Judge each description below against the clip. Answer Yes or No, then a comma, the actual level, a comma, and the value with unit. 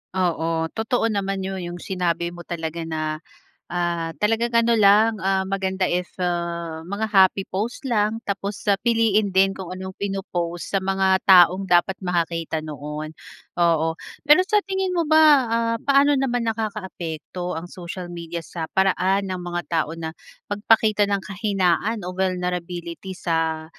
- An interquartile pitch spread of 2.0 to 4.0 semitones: Yes, average, 3.3 semitones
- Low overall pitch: No, high, 190 Hz